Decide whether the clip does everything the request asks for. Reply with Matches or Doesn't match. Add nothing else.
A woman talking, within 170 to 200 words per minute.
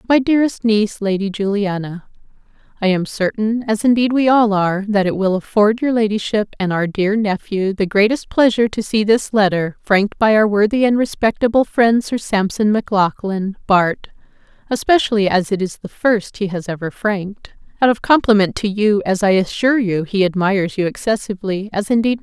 Matches